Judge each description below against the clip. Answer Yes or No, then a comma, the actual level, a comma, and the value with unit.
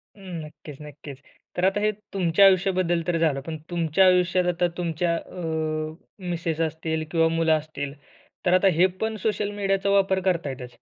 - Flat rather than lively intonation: No, average, 3.0 semitones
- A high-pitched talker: No, medium, 175 Hz